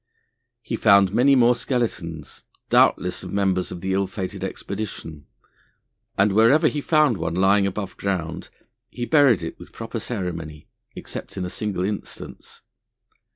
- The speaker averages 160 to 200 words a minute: No, average, 145 wpm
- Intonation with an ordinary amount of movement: Yes, average, 4.2 semitones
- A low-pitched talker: Yes, low, 100 Hz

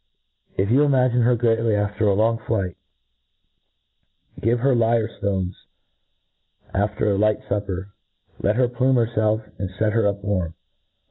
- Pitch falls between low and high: No, low, 110 Hz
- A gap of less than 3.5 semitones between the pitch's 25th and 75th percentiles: Yes, average, 2.7 semitones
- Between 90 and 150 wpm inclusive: Yes, average, 140 wpm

